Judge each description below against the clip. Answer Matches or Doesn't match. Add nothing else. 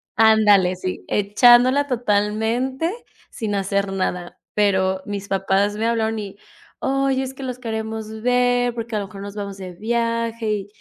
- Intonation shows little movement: Doesn't match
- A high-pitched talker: Matches